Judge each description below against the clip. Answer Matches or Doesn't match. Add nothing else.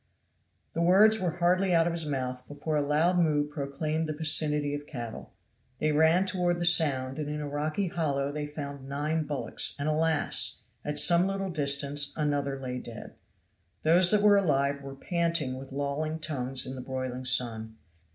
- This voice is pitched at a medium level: Matches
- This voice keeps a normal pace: Matches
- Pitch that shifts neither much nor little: Matches